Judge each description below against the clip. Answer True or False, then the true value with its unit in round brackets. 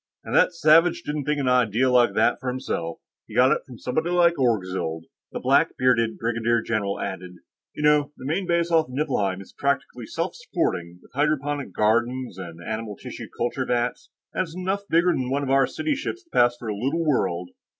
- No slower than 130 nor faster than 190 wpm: False (200 wpm)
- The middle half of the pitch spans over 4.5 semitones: True (5.4 semitones)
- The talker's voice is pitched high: False (125 Hz)